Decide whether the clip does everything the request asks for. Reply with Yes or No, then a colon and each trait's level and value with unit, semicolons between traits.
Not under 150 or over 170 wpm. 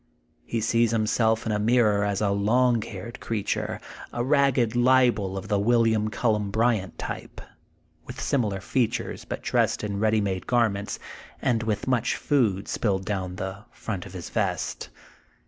Yes: average, 155 wpm